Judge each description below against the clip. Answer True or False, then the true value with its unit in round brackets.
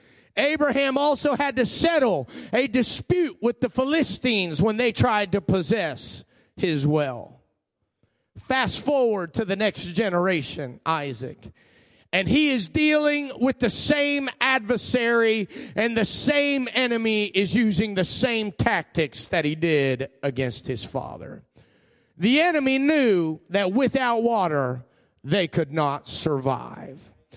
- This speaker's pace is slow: True (125 wpm)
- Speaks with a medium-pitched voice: False (220 Hz)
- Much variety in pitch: True (8.3 semitones)